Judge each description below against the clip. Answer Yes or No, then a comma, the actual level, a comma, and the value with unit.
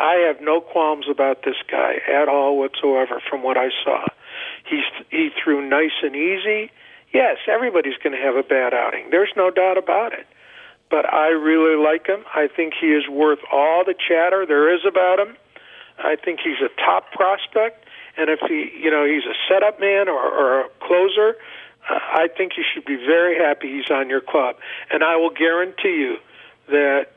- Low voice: No, medium, 170 Hz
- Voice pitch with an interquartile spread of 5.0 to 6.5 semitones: Yes, average, 5.3 semitones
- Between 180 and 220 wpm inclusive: Yes, average, 190 wpm